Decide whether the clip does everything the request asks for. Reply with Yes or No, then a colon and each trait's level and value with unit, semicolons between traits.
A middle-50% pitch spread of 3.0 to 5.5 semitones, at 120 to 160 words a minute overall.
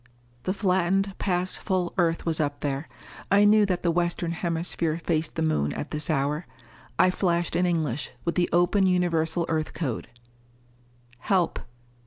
No: narrow, 2.4 semitones; average, 155 wpm